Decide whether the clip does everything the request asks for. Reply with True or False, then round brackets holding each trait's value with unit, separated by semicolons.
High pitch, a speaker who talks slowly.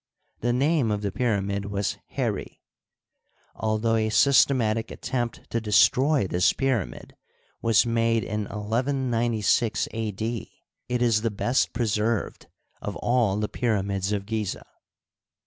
False (110 Hz; 130 wpm)